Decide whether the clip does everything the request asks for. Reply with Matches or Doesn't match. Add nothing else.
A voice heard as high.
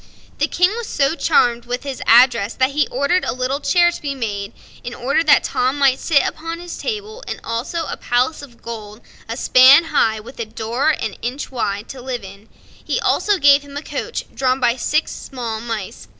Matches